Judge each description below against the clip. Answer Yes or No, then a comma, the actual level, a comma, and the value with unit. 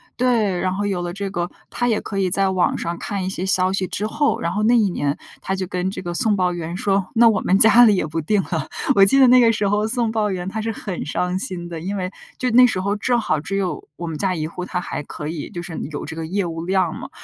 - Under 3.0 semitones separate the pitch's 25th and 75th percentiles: No, average, 3.3 semitones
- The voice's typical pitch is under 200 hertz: Yes, high, 190 Hz